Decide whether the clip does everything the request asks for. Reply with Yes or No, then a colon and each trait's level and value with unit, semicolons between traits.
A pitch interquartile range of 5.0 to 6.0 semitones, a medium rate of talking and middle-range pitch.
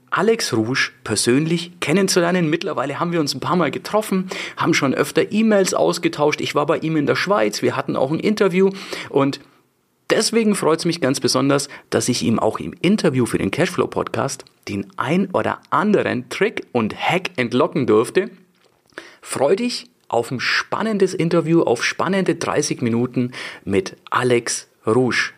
Yes: wide, 5.6 semitones; average, 160 wpm; medium, 170 Hz